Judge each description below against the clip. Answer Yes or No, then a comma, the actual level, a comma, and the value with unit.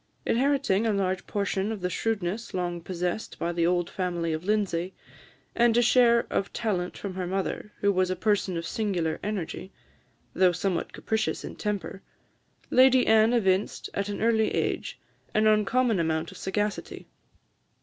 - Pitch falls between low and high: No, high, 195 Hz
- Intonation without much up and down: No, average, 3.6 semitones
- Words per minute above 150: Yes, average, 160 wpm